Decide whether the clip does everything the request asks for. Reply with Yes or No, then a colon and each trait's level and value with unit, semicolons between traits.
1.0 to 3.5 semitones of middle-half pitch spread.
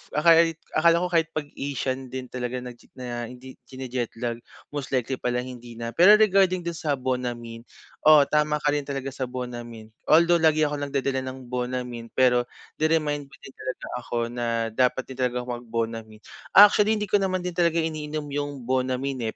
No: average, 4.0 semitones